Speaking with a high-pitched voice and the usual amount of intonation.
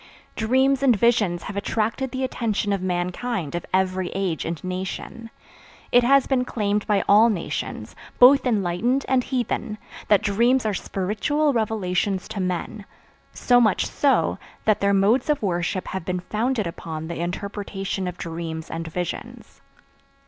Yes: high, 205 Hz; average, 4.8 semitones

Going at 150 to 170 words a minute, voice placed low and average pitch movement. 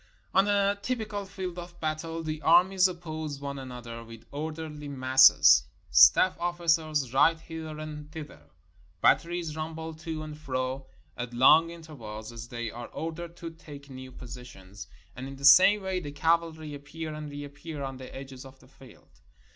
No: average, 165 wpm; medium, 155 Hz; average, 3.8 semitones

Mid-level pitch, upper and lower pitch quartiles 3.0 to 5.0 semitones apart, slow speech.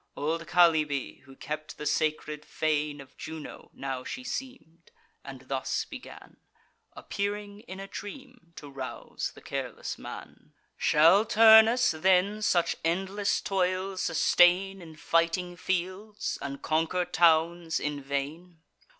Yes: medium, 170 Hz; average, 4.3 semitones; slow, 125 wpm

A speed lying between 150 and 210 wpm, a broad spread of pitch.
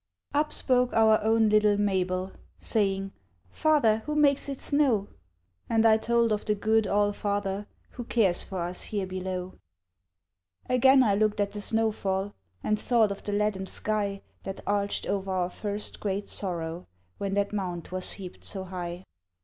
No: average, 165 wpm; narrow, 2.6 semitones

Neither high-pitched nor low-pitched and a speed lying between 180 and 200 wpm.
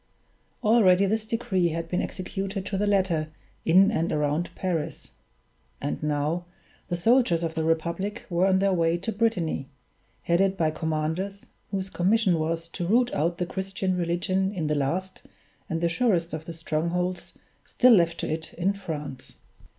No: medium, 175 Hz; average, 160 wpm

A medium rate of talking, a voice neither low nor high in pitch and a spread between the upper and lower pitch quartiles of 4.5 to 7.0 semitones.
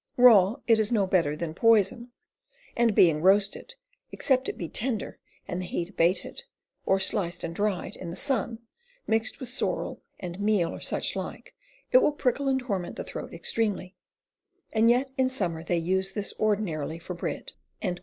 No: average, 170 wpm; high, 205 Hz; average, 4.9 semitones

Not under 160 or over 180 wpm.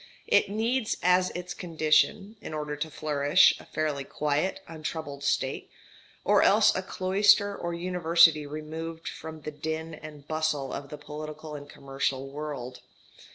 No: average, 145 wpm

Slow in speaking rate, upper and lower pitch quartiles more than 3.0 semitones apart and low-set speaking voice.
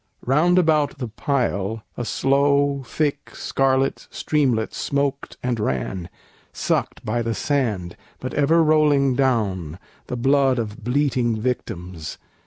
Yes: slow, 120 wpm; average, 4.3 semitones; low, 130 Hz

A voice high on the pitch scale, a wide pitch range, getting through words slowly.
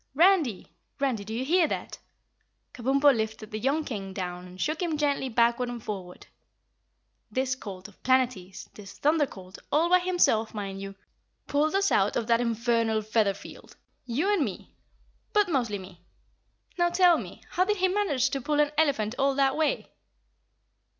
No: very high, 255 Hz; wide, 6.3 semitones; average, 170 wpm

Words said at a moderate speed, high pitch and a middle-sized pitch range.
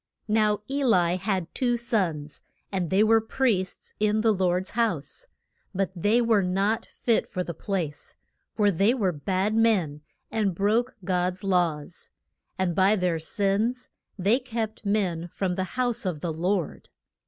Yes: average, 155 wpm; high, 195 Hz; average, 3.7 semitones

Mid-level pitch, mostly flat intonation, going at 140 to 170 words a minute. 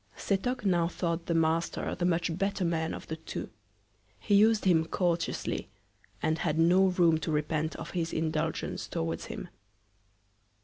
Yes: medium, 170 Hz; narrow, 2.2 semitones; average, 150 wpm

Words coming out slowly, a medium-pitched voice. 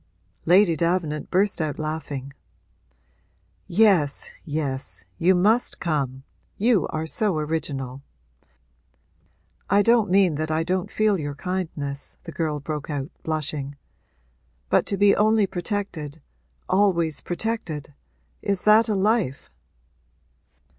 Yes: slow, 115 wpm; medium, 165 Hz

